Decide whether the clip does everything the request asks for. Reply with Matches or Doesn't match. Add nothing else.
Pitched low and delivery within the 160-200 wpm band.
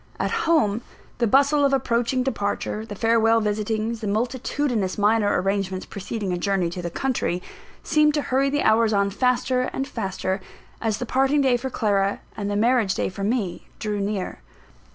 Doesn't match